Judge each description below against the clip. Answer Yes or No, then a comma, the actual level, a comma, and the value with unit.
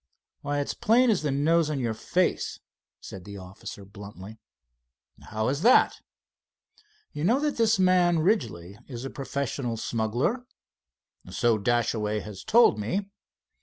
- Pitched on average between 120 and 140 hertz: Yes, low, 135 Hz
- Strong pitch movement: Yes, wide, 9.0 semitones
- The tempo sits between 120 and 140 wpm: Yes, slow, 135 wpm